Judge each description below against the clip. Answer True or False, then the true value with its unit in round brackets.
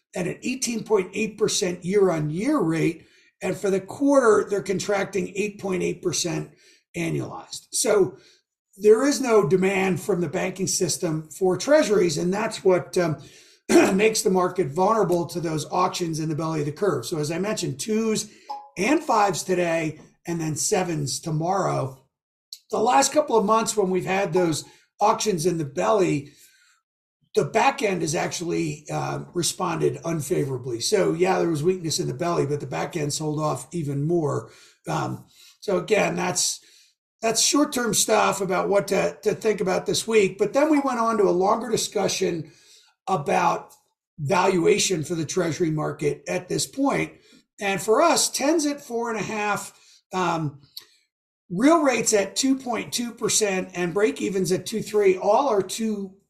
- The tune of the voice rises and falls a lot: False (4.1 semitones)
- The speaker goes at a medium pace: True (160 wpm)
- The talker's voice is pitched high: True (195 Hz)